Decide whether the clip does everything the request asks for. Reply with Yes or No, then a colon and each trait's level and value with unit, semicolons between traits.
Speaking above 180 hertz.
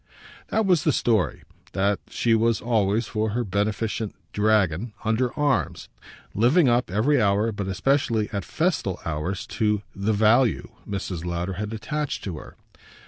No: low, 110 Hz